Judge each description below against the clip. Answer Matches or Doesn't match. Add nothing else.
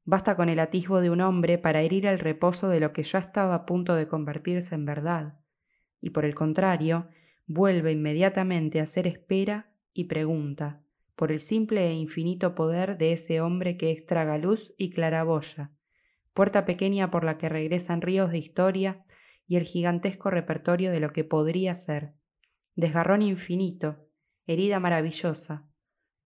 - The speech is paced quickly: Doesn't match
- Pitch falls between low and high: Matches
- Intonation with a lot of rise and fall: Doesn't match